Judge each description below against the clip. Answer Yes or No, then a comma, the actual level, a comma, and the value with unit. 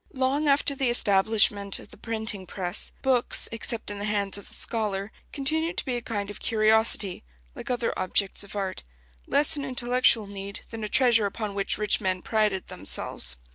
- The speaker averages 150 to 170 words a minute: No, average, 180 wpm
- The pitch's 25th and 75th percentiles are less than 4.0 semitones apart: Yes, average, 3.4 semitones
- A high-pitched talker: Yes, high, 215 Hz